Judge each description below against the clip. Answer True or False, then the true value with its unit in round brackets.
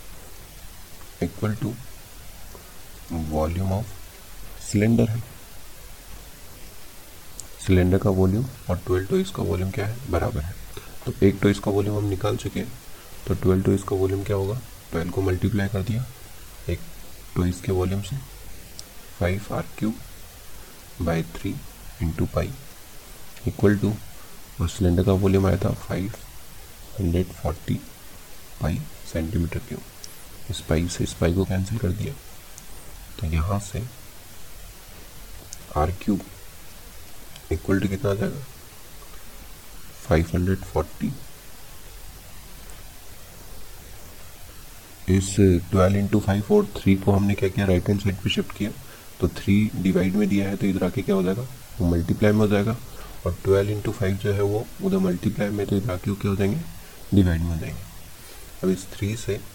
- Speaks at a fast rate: False (130 wpm)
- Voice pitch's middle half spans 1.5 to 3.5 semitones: True (2.9 semitones)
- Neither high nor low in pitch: False (95 Hz)